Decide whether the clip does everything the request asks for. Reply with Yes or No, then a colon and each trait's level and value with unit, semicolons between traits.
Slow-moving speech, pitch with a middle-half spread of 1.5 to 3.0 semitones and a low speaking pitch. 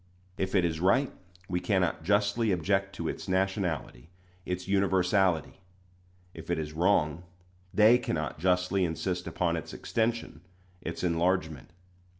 Yes: slow, 130 wpm; average, 2.7 semitones; very low, 90 Hz